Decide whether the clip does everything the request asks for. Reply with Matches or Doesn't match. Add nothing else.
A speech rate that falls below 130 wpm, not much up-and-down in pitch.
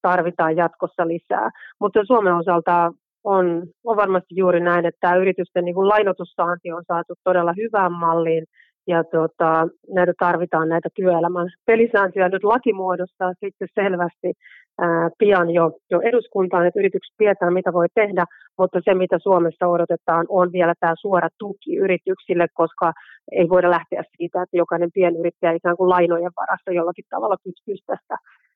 Doesn't match